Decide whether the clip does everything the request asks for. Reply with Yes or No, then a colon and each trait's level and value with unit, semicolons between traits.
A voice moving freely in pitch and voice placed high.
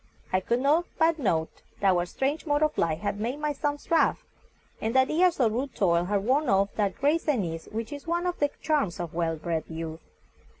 Yes: wide, 8.9 semitones; high, 235 Hz